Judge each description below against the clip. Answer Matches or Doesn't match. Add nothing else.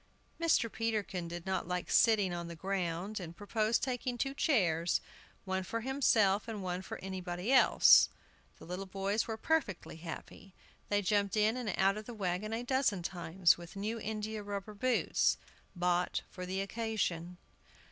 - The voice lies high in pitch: Matches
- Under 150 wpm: Doesn't match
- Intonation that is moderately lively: Matches